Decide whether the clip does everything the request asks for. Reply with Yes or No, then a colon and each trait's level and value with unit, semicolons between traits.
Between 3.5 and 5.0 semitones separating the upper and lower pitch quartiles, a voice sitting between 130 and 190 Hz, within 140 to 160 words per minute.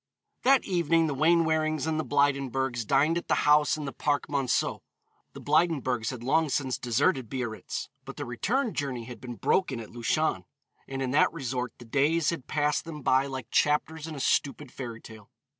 No: average, 3.8 semitones; medium, 140 Hz; average, 185 wpm